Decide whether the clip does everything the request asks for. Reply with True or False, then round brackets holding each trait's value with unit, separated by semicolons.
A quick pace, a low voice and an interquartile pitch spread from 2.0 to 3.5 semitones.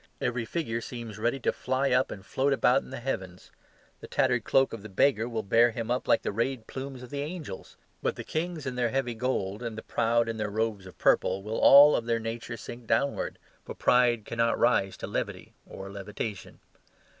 True (210 wpm; 115 Hz; 3.0 semitones)